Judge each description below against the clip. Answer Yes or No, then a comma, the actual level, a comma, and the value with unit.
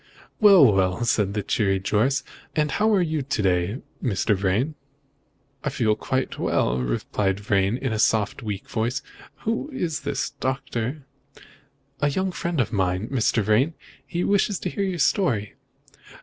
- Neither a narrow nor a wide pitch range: No, wide, 7.1 semitones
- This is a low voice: Yes, low, 120 Hz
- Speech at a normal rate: Yes, average, 155 wpm